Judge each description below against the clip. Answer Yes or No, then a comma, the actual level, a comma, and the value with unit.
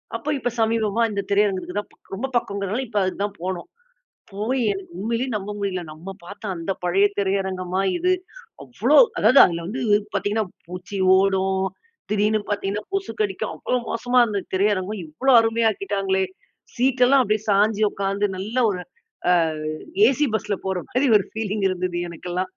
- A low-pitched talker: No, high, 200 Hz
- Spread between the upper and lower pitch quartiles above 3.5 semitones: No, average, 2.8 semitones